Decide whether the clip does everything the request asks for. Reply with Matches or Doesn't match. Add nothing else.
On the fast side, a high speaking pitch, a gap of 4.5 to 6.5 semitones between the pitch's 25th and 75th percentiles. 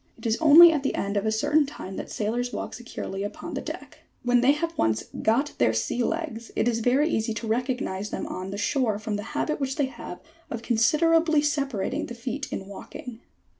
Matches